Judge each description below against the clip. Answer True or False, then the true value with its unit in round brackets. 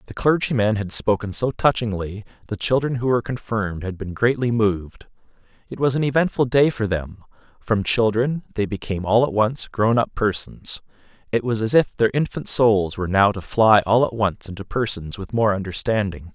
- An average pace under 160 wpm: False (185 wpm)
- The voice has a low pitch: True (110 Hz)